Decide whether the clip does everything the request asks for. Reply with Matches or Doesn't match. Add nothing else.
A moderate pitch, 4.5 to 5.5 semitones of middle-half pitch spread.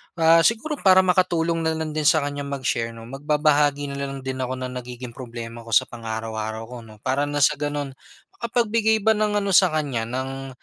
Matches